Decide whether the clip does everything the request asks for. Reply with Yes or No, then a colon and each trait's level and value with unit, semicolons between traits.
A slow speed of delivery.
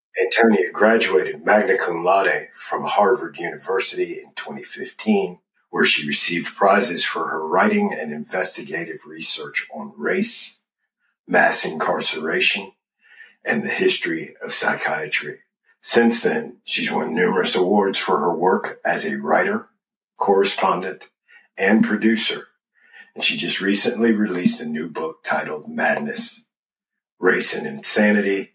Yes: slow, 120 wpm